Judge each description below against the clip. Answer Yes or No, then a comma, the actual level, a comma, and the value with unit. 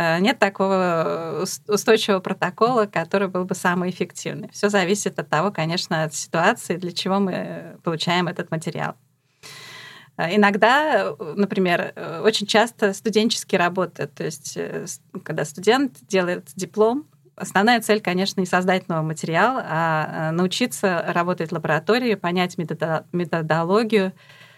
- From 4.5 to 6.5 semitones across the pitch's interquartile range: No, average, 3.7 semitones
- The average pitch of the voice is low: No, medium, 185 Hz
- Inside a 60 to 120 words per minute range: Yes, average, 115 wpm